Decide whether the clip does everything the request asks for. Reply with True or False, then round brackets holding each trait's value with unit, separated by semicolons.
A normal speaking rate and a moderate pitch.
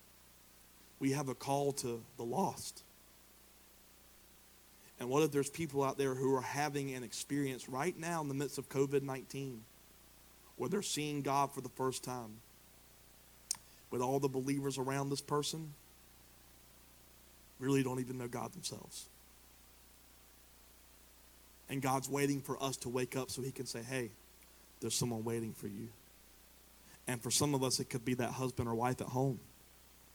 False (160 wpm; 125 Hz)